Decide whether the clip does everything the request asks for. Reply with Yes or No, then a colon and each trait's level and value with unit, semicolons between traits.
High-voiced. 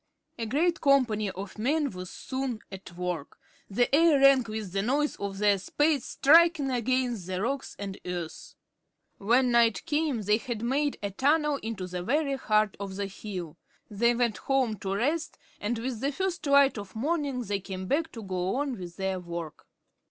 Yes: high, 230 Hz